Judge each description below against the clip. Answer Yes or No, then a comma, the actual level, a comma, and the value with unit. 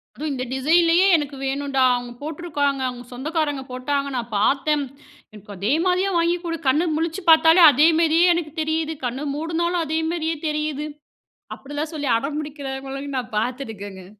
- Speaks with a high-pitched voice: Yes, very high, 290 Hz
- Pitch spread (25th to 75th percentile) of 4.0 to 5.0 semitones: No, average, 3.4 semitones